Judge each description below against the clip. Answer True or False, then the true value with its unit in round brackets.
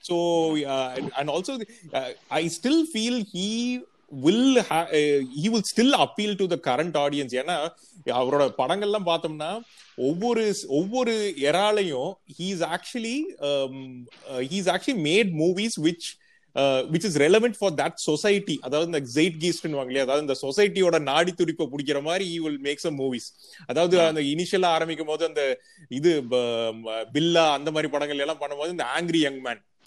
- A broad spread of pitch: True (6.2 semitones)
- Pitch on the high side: False (165 Hz)